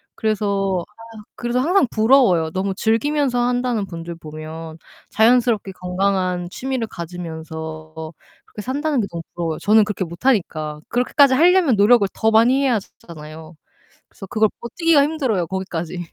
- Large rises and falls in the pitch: Yes, wide, 6.4 semitones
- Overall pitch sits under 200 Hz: No, high, 205 Hz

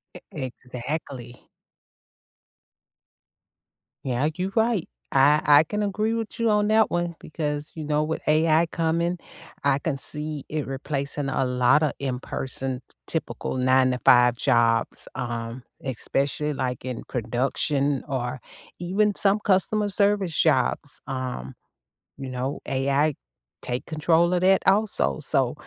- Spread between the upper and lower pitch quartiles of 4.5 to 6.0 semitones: Yes, average, 4.9 semitones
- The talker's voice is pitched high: No, medium, 145 Hz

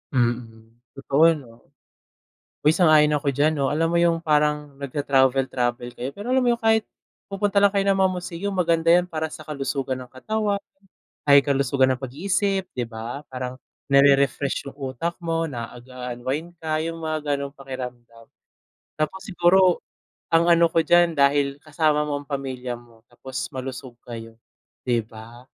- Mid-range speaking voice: Yes, medium, 145 Hz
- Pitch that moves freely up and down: No, average, 4.6 semitones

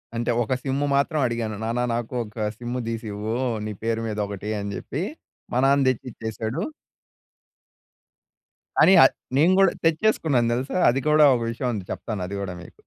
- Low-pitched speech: Yes, low, 120 Hz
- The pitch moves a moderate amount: Yes, average, 4.0 semitones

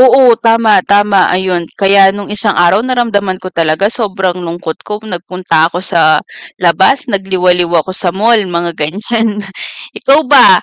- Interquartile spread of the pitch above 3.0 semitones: Yes, average, 3.7 semitones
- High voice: Yes, high, 195 Hz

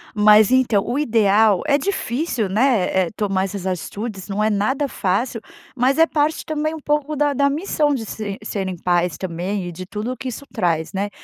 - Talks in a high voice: Yes, high, 220 Hz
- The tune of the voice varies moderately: No, wide, 6.2 semitones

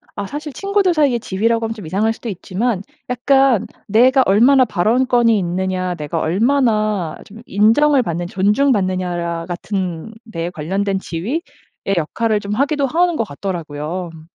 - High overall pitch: Yes, high, 210 Hz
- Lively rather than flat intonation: Yes, wide, 5.7 semitones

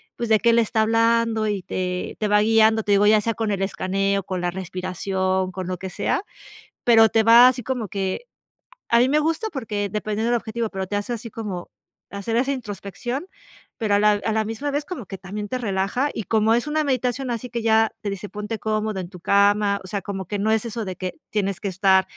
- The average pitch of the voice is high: Yes, high, 215 Hz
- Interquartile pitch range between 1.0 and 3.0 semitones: Yes, average, 2.7 semitones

